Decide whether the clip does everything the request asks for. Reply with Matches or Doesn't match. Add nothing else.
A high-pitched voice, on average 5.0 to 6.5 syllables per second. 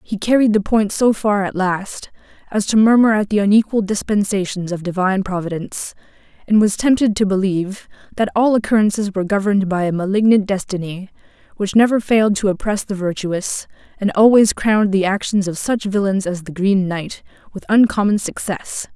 Matches